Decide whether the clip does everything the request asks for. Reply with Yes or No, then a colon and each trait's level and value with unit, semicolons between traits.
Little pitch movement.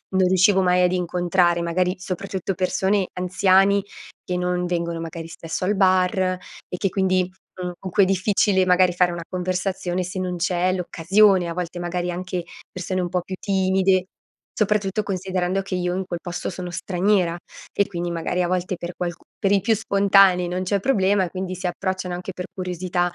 Yes: narrow, 1.2 semitones